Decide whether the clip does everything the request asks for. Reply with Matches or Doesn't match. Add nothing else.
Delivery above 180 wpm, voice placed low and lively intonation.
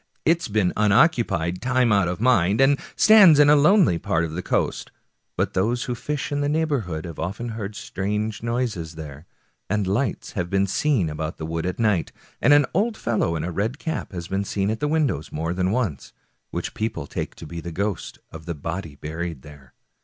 Matches